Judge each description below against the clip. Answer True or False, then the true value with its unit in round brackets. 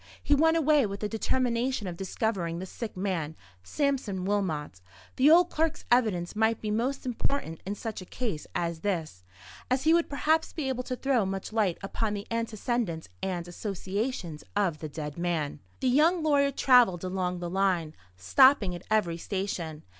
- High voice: True (205 Hz)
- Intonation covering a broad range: True (6.6 semitones)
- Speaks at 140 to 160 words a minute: False (170 wpm)